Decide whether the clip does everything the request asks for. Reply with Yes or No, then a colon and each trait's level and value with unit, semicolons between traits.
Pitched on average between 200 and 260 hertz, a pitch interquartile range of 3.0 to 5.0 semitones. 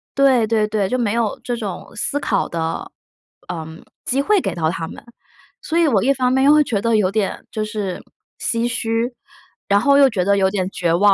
Yes: high, 220 Hz; average, 4.6 semitones